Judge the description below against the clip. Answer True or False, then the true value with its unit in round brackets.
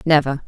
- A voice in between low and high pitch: True (145 Hz)